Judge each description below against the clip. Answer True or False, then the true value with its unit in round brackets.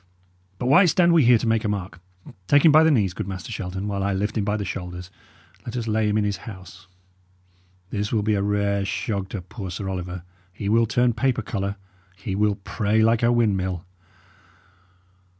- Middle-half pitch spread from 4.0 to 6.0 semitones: False (3.0 semitones)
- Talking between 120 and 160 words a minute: False (205 wpm)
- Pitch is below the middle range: True (105 Hz)